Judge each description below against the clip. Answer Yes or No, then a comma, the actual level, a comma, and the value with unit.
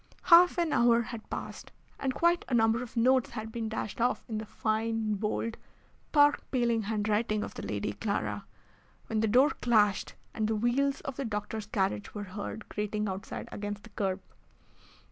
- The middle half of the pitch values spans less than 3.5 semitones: Yes, narrow, 2.6 semitones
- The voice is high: Yes, high, 225 Hz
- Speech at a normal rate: Yes, average, 175 wpm